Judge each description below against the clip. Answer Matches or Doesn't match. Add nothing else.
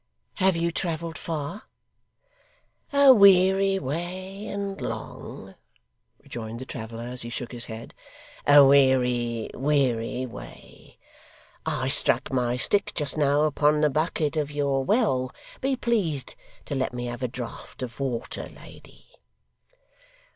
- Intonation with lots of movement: Matches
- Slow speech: Matches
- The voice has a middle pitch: Matches